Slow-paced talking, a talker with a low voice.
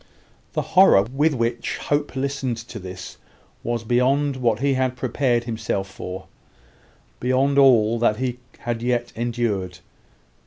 Yes: slow, 130 wpm; low, 120 Hz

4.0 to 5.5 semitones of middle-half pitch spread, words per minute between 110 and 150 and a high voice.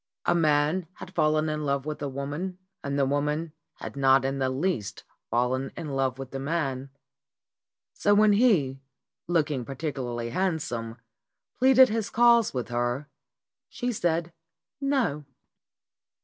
No: average, 4.6 semitones; average, 140 wpm; medium, 145 Hz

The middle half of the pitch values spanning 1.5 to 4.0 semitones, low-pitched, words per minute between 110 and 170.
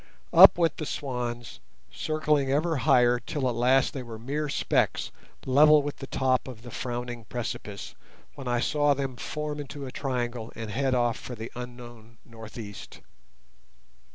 Yes: average, 3.0 semitones; low, 125 Hz; average, 160 wpm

